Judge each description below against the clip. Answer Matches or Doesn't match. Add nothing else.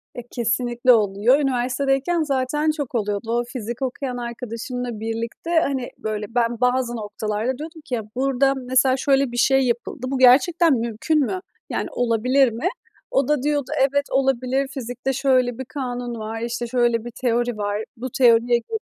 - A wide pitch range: Doesn't match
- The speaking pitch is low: Doesn't match